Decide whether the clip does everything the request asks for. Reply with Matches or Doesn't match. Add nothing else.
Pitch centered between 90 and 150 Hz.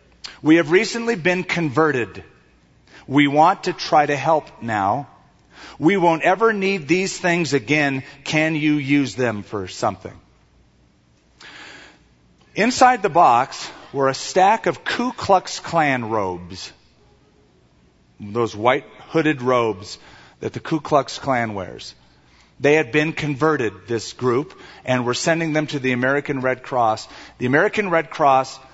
Matches